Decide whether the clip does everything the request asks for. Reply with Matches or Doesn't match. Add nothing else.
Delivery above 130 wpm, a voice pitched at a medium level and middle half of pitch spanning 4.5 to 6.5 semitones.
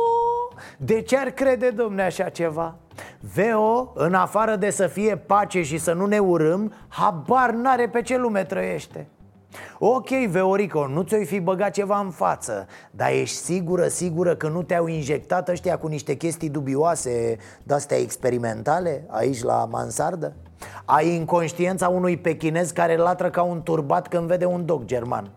Matches